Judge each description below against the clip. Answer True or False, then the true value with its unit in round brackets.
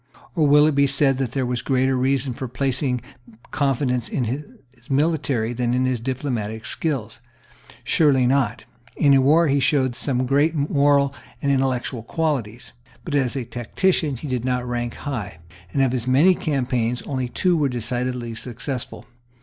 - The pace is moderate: True (160 wpm)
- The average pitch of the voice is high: False (130 Hz)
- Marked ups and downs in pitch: False (2.4 semitones)